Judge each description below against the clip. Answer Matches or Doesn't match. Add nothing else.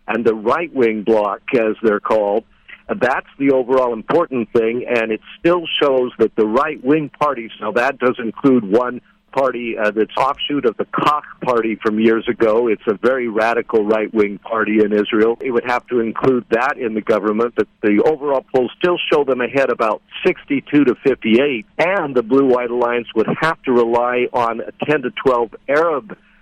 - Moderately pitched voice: Doesn't match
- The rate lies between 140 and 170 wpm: Doesn't match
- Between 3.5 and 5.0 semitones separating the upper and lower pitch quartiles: Doesn't match